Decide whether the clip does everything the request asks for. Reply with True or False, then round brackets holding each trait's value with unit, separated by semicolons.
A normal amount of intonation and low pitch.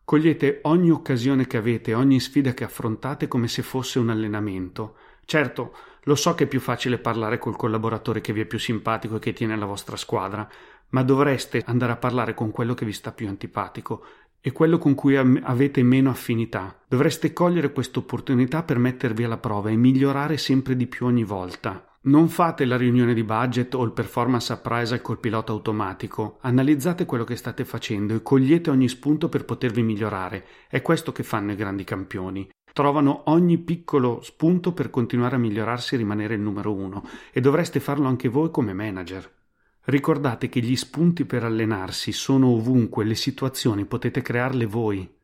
True (3.5 semitones; 125 Hz)